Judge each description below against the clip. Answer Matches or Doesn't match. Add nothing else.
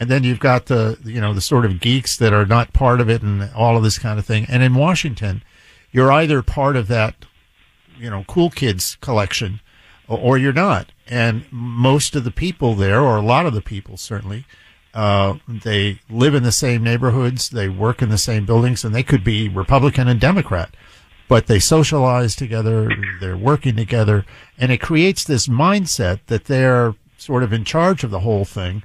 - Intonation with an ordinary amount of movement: Matches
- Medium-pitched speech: Doesn't match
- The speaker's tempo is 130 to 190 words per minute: Doesn't match